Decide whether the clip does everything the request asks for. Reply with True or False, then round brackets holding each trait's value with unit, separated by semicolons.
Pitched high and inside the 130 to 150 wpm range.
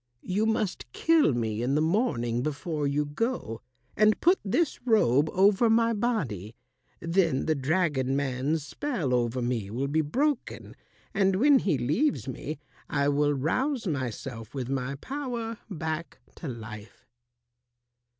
False (155 Hz; 140 wpm)